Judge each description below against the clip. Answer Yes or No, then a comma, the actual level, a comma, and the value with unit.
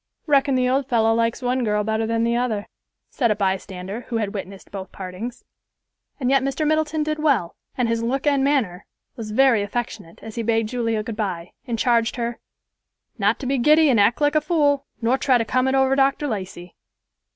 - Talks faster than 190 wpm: Yes, fast, 205 wpm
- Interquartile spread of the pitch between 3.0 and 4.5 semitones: Yes, average, 4.1 semitones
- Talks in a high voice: Yes, high, 235 Hz